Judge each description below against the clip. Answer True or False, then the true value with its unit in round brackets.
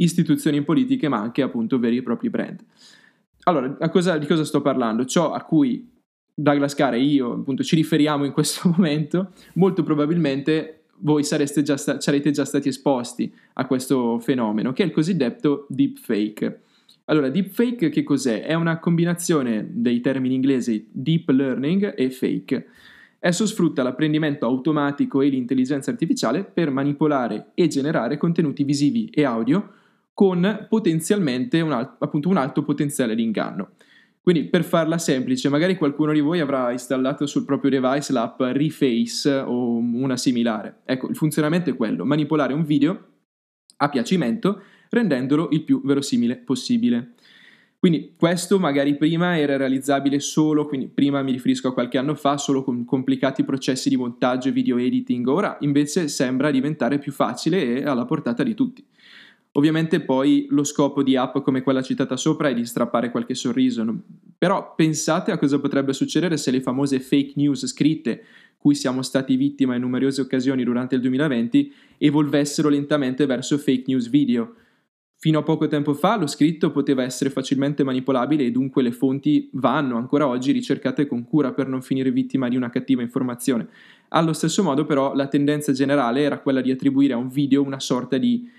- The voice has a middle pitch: True (145 Hz)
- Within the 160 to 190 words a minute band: True (165 wpm)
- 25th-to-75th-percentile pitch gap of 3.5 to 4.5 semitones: True (3.8 semitones)